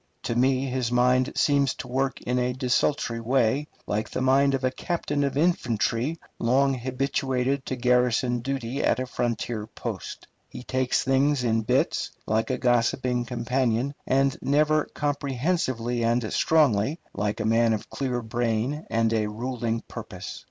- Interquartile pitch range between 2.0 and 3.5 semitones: Yes, narrow, 2.6 semitones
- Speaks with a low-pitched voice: Yes, low, 125 Hz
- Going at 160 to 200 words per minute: No, average, 150 wpm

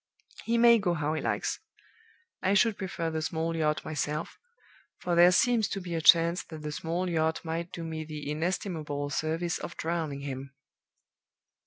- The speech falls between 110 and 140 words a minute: No, average, 170 wpm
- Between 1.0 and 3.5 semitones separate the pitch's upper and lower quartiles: Yes, narrow, 2.5 semitones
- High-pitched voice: No, medium, 165 Hz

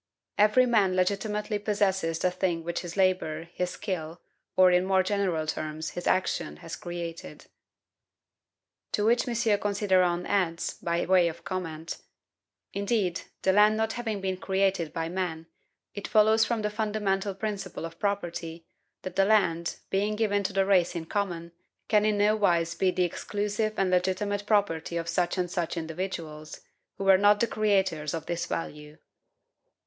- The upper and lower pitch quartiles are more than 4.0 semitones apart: No, average, 3.3 semitones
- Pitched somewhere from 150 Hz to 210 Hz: Yes, high, 190 Hz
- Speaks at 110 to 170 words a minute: Yes, average, 160 wpm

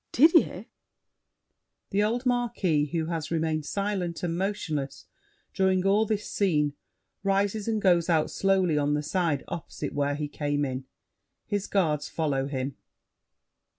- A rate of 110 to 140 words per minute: Yes, slow, 135 wpm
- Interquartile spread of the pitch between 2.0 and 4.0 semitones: No, average, 5.1 semitones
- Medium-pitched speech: Yes, medium, 170 Hz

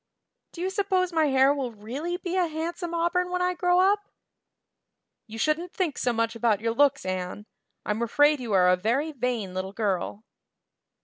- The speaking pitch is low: No, very high, 285 Hz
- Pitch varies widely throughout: Yes, wide, 7.8 semitones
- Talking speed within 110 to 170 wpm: No, average, 180 wpm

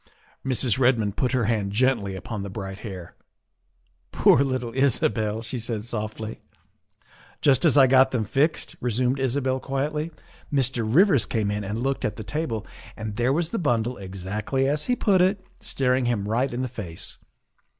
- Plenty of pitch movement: No, average, 3.9 semitones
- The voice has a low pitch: Yes, low, 125 Hz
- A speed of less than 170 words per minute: No, average, 175 wpm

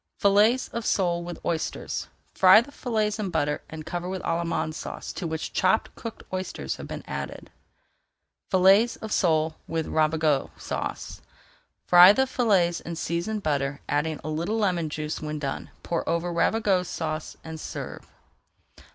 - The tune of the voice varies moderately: Yes, average, 4.2 semitones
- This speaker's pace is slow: No, average, 150 wpm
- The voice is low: No, medium, 170 Hz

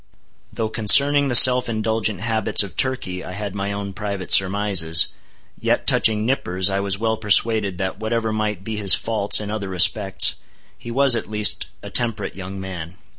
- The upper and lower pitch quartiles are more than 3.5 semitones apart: No, narrow, 2.6 semitones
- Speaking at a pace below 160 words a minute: No, average, 175 wpm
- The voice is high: No, low, 105 Hz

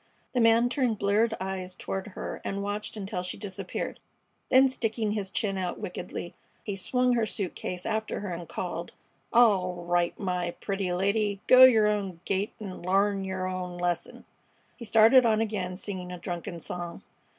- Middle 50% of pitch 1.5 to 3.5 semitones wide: Yes, average, 3.2 semitones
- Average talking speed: Yes, average, 170 wpm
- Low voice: No, high, 195 Hz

